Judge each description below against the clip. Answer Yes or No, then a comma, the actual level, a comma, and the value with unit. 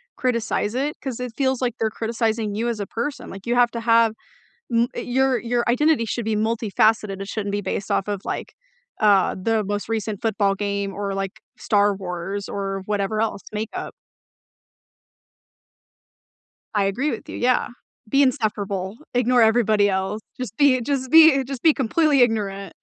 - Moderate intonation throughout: Yes, average, 3.3 semitones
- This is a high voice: Yes, high, 220 Hz